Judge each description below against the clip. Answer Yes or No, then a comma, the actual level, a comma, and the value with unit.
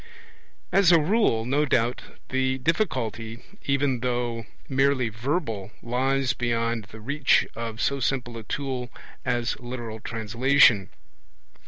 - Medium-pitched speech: No, low, 125 Hz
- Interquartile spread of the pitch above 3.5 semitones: No, average, 3.0 semitones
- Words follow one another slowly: Yes, slow, 120 wpm